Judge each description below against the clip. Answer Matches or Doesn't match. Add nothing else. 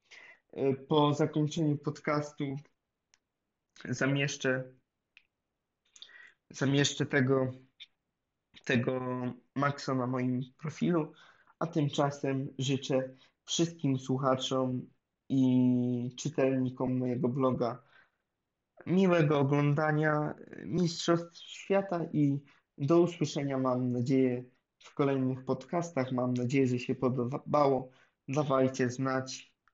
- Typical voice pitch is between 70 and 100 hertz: Doesn't match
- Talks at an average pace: Doesn't match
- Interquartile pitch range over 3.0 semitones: Doesn't match